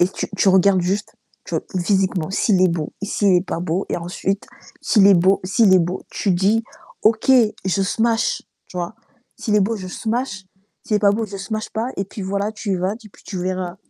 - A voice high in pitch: Yes, high, 195 Hz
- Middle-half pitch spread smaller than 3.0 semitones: Yes, narrow, 2.6 semitones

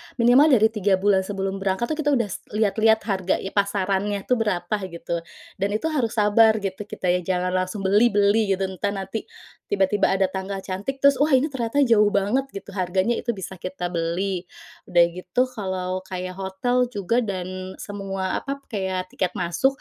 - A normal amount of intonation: Yes, average, 3.1 semitones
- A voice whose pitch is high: Yes, high, 200 Hz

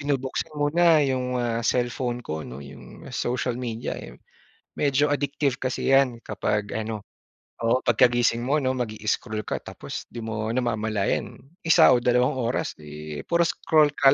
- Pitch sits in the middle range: No, low, 125 Hz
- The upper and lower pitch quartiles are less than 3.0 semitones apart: No, average, 3.6 semitones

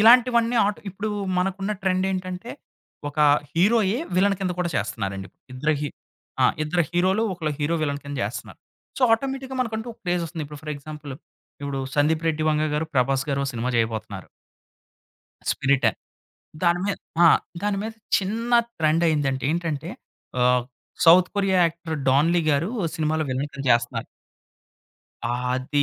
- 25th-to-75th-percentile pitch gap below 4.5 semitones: No, average, 5.2 semitones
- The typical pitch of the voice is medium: Yes, medium, 160 Hz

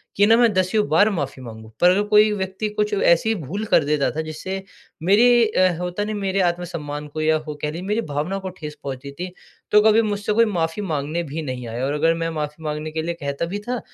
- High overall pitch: No, medium, 170 Hz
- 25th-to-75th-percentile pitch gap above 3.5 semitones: Yes, wide, 5.4 semitones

